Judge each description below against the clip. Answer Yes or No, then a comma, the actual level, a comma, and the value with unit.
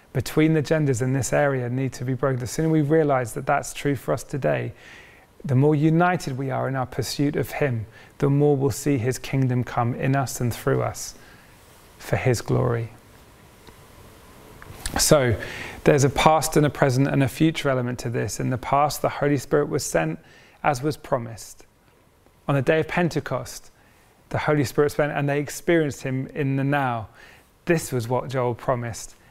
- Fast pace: No, average, 185 wpm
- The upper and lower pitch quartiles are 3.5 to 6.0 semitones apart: No, average, 2.8 semitones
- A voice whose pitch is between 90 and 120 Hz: No, low, 135 Hz